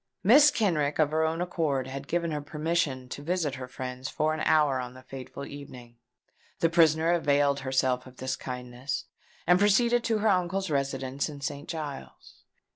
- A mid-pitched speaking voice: Yes, medium, 145 Hz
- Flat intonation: No, average, 4.2 semitones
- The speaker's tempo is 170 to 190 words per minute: Yes, average, 175 wpm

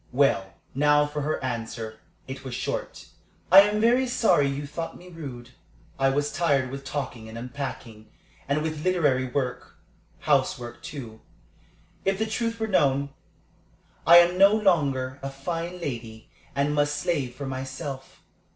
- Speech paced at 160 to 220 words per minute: No, average, 150 wpm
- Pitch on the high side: No, medium, 140 Hz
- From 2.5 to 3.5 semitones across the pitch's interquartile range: No, average, 4.7 semitones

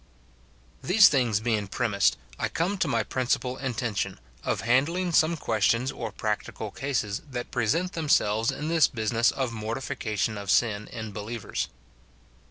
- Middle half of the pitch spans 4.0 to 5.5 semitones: Yes, average, 4.5 semitones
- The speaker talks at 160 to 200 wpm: No, average, 140 wpm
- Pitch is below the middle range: Yes, low, 120 Hz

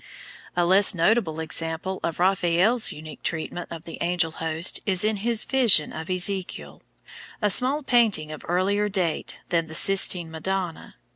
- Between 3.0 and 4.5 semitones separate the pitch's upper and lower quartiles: Yes, average, 3.7 semitones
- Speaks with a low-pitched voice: No, medium, 180 Hz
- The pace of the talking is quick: No, average, 150 wpm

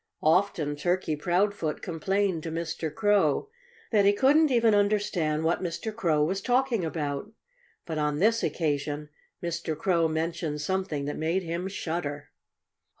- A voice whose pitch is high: No, medium, 170 Hz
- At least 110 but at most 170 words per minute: Yes, average, 140 wpm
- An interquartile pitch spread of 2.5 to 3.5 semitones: No, average, 4.7 semitones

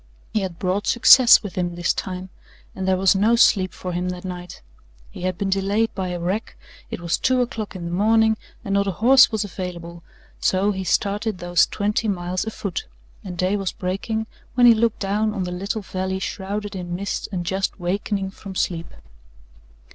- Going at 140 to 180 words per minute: No, average, 195 wpm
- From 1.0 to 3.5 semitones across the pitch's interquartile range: Yes, narrow, 2.5 semitones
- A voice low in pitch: No, high, 190 Hz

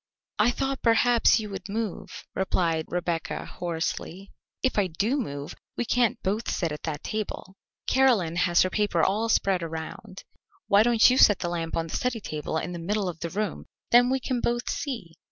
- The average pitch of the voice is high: Yes, high, 195 Hz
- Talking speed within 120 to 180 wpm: No, average, 190 wpm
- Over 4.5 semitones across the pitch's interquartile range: Yes, average, 5.3 semitones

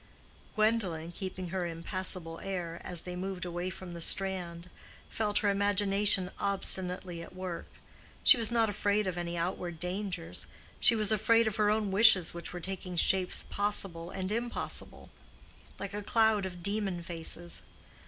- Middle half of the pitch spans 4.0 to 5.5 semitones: No, average, 2.9 semitones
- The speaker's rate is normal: Yes, average, 150 wpm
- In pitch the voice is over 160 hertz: Yes, high, 190 Hz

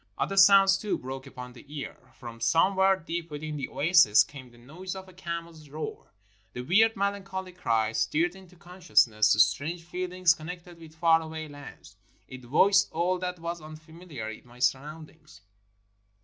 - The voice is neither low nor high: Yes, medium, 165 Hz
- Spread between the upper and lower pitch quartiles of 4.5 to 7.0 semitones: Yes, average, 4.9 semitones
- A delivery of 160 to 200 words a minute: Yes, average, 165 wpm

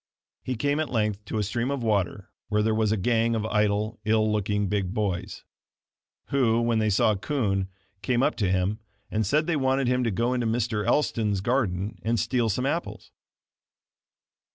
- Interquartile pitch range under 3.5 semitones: Yes, average, 2.9 semitones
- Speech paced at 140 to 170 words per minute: No, average, 180 wpm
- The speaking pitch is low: Yes, low, 110 Hz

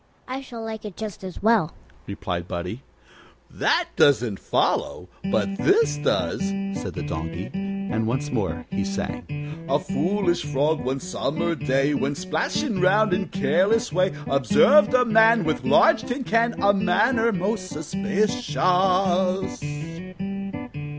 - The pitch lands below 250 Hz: Yes, medium, 185 Hz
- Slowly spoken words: Yes, slow, 130 wpm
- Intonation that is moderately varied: No, wide, 5.8 semitones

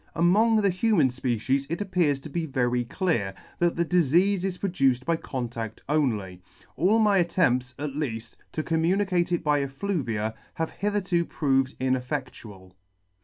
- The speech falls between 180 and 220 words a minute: No, average, 150 wpm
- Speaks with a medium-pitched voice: Yes, medium, 150 Hz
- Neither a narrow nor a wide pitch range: No, wide, 6.1 semitones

